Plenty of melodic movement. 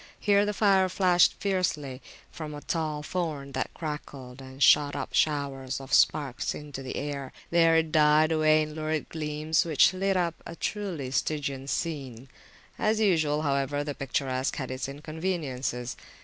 No: average, 3.3 semitones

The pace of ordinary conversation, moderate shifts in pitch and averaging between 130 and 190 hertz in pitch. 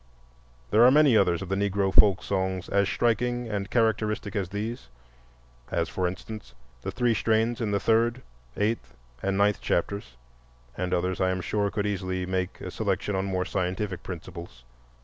No: average, 170 wpm; average, 3.0 semitones; low, 100 Hz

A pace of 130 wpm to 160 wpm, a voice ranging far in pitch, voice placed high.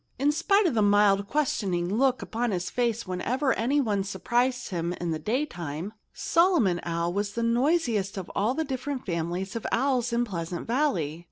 No: average, 170 wpm; wide, 6.1 semitones; high, 220 Hz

